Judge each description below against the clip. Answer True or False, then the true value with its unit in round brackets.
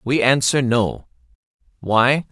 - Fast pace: False (105 wpm)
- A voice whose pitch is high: False (125 Hz)